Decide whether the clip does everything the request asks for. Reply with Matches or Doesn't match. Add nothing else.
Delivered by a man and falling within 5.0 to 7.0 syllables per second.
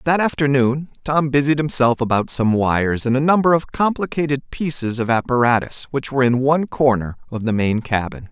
Matches